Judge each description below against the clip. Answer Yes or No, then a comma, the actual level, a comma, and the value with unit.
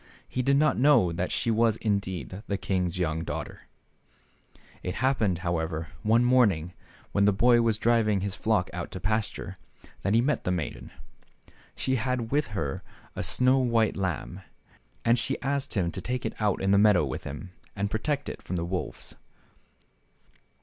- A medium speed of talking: Yes, average, 175 wpm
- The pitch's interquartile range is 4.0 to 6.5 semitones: Yes, average, 4.8 semitones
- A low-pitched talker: Yes, low, 105 Hz